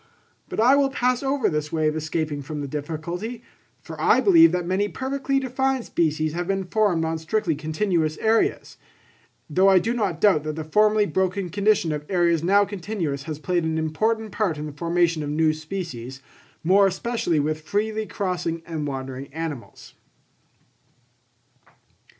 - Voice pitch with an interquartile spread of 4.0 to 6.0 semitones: Yes, average, 5.3 semitones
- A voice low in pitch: No, medium, 175 Hz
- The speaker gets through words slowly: No, average, 160 wpm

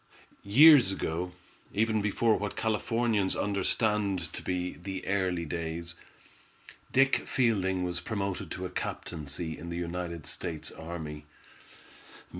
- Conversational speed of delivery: No, slow, 115 wpm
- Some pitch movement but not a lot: Yes, average, 3.6 semitones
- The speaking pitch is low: Yes, very low, 90 Hz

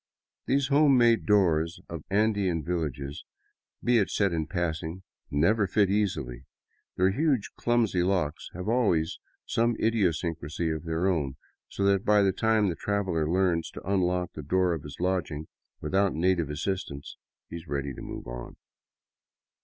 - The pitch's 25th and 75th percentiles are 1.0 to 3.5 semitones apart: No, average, 4.2 semitones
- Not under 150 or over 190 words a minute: Yes, average, 155 wpm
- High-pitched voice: No, very low, 90 Hz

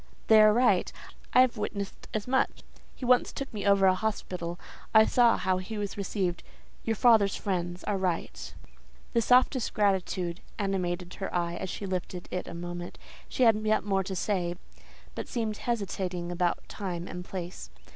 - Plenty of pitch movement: No, average, 3.4 semitones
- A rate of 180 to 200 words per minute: No, average, 170 wpm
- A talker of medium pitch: No, high, 195 Hz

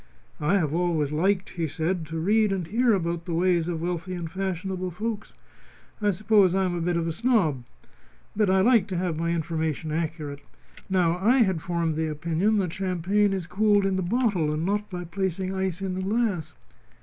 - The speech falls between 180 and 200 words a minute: Yes, average, 195 wpm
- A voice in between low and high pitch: Yes, medium, 180 Hz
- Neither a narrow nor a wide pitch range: Yes, average, 3.0 semitones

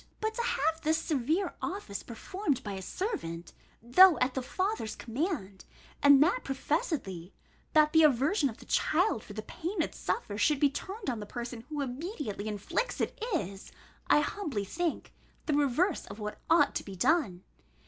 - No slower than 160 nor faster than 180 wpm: Yes, average, 170 wpm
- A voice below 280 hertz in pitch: No, very high, 285 Hz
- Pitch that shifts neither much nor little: No, wide, 7.9 semitones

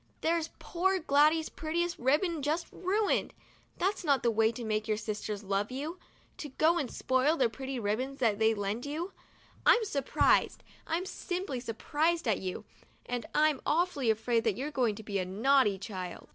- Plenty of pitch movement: Yes, wide, 6.7 semitones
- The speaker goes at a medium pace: Yes, average, 175 wpm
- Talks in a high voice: Yes, very high, 265 Hz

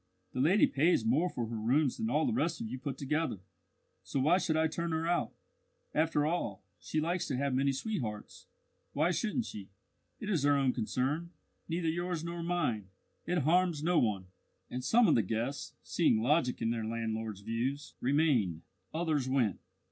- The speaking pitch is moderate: Yes, medium, 145 Hz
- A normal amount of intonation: No, wide, 6.1 semitones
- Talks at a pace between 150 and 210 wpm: Yes, average, 185 wpm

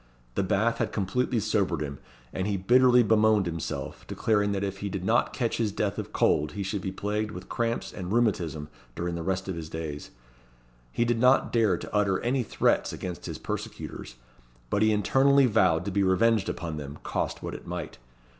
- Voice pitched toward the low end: Yes, low, 100 Hz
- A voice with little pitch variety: No, average, 3.8 semitones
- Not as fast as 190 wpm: No, average, 195 wpm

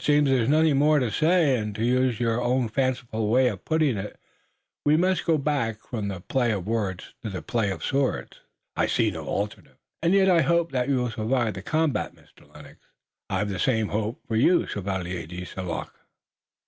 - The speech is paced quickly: Yes, fast, 210 wpm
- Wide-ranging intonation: Yes, wide, 5.7 semitones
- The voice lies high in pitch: No, low, 120 Hz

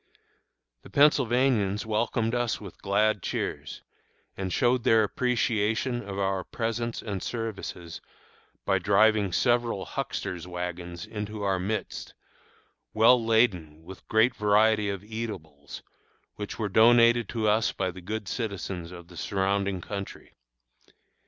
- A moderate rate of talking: No, slow, 125 wpm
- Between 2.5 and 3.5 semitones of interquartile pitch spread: Yes, average, 3.1 semitones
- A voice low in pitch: Yes, low, 105 Hz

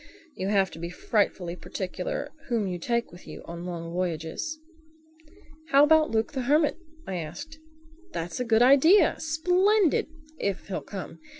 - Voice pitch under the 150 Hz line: No, high, 225 Hz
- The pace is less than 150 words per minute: Yes, average, 140 wpm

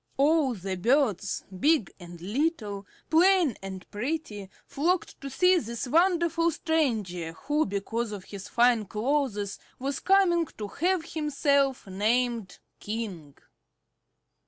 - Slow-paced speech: Yes, slow, 115 wpm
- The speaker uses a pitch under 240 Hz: No, high, 245 Hz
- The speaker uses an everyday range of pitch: No, wide, 7.8 semitones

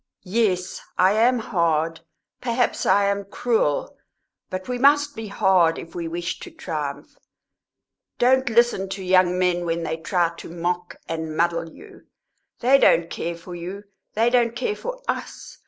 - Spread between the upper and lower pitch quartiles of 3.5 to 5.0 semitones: No, wide, 5.6 semitones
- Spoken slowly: No, average, 155 wpm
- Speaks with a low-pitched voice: No, medium, 185 Hz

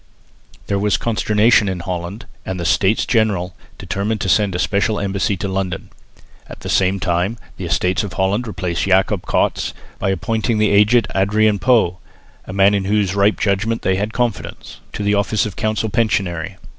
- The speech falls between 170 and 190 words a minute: Yes, average, 175 wpm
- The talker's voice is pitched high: No, low, 100 Hz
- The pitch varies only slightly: Yes, narrow, 2.3 semitones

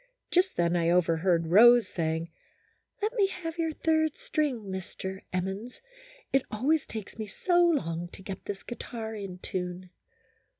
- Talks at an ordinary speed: Yes, average, 155 wpm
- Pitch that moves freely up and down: Yes, wide, 9.0 semitones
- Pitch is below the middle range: No, high, 205 Hz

